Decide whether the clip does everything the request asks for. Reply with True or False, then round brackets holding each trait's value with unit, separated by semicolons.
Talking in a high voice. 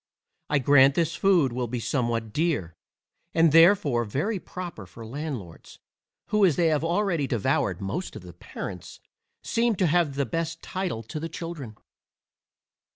False (150 Hz)